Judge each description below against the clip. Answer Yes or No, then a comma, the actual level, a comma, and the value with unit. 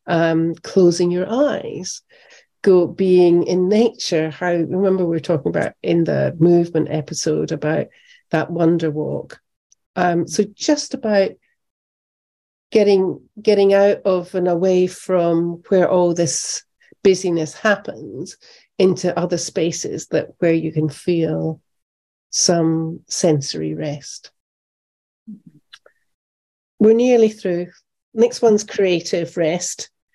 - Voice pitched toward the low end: No, medium, 175 Hz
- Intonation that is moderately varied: Yes, average, 3.5 semitones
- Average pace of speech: No, slow, 110 wpm